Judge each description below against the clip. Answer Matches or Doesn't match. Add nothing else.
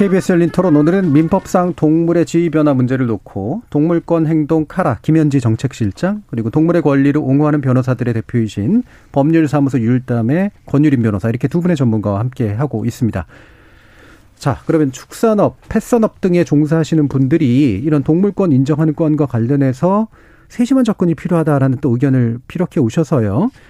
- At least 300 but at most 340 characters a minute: Doesn't match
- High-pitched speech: Doesn't match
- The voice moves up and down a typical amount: Matches